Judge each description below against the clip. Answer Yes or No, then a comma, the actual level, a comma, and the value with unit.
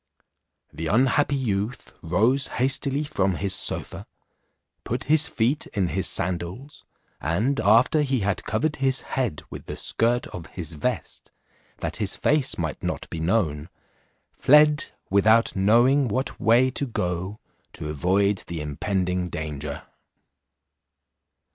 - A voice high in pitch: No, low, 105 Hz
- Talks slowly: Yes, slow, 130 wpm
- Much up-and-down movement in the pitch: Yes, wide, 7.0 semitones